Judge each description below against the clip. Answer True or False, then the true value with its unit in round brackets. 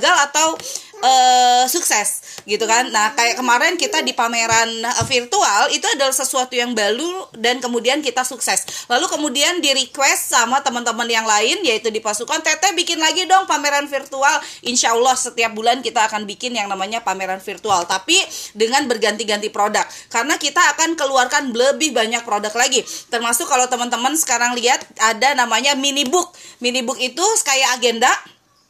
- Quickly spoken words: True (155 wpm)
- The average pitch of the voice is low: False (255 Hz)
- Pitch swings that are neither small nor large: True (4.6 semitones)